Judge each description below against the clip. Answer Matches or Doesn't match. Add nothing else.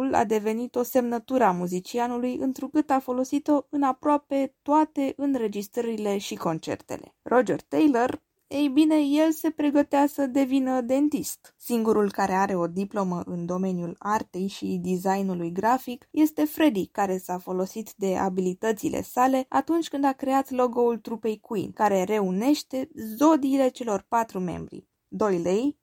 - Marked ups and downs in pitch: Matches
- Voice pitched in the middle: Doesn't match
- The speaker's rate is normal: Matches